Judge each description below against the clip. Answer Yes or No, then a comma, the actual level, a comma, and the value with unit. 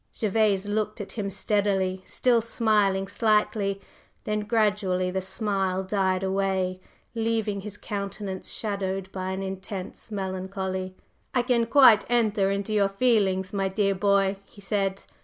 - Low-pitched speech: No, high, 200 Hz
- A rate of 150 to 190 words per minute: No, slow, 135 wpm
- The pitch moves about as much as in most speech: No, narrow, 1.9 semitones